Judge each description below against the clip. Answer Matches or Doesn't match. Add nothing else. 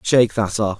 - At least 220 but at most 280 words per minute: Matches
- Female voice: Doesn't match